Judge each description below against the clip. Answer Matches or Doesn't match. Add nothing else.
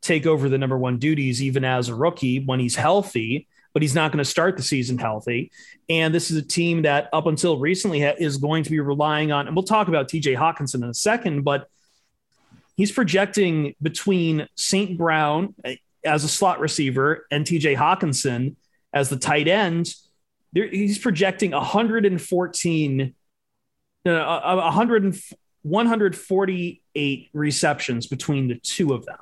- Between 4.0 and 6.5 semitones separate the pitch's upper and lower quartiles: Matches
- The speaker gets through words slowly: Doesn't match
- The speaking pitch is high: Doesn't match